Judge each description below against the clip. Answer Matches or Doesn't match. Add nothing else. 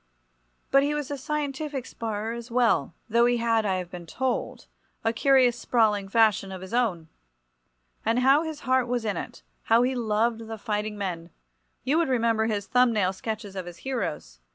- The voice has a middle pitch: Doesn't match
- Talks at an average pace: Matches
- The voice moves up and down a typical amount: Matches